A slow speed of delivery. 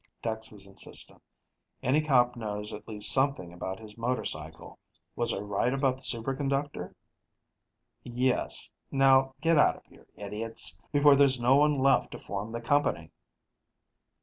No: average, 145 wpm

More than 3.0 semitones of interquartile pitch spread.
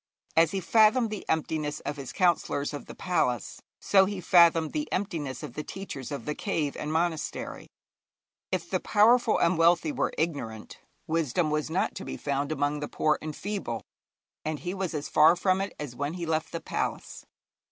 Yes: average, 4.0 semitones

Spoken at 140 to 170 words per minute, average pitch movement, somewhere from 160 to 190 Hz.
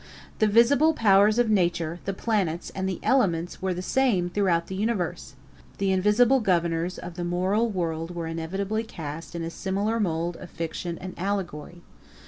Yes: average, 165 wpm; average, 3.6 semitones; medium, 185 Hz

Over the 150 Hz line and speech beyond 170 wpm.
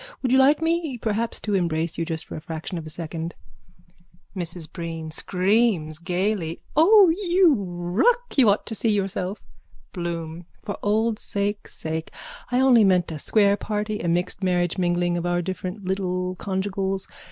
No: high, 190 Hz; average, 165 wpm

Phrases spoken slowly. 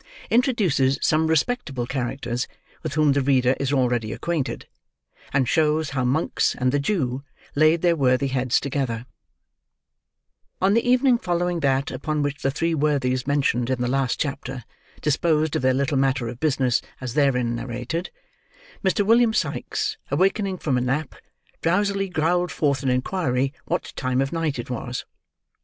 No: average, 155 wpm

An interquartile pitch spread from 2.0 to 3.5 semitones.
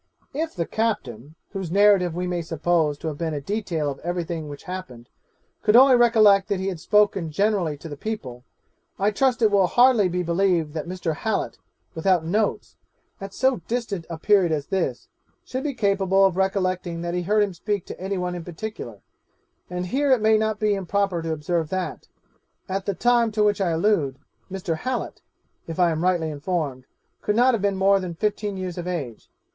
No: average, 4.0 semitones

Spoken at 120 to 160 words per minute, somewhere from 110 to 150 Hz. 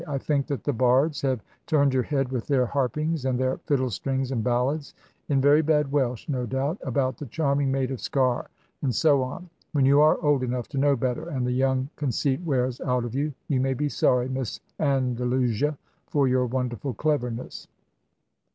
No: average, 190 wpm; low, 135 Hz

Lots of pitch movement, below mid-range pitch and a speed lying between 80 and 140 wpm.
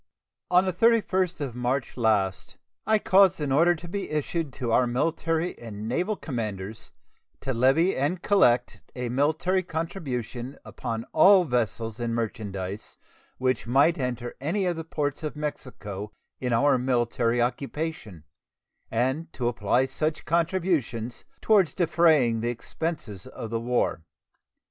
Yes: wide, 5.9 semitones; low, 130 Hz; slow, 135 wpm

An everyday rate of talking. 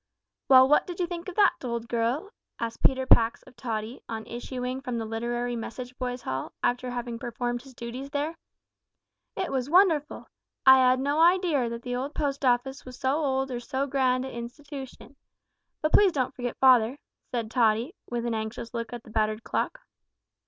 Yes: average, 180 wpm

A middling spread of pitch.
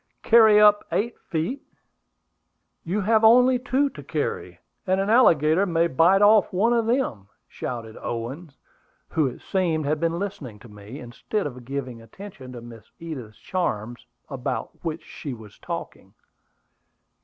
No: wide, 8.9 semitones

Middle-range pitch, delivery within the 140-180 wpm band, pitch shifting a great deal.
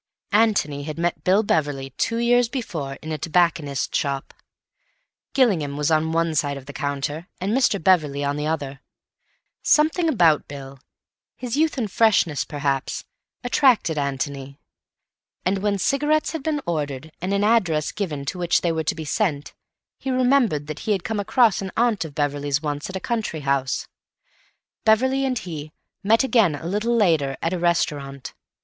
Yes: medium, 165 Hz; average, 170 wpm; wide, 7.3 semitones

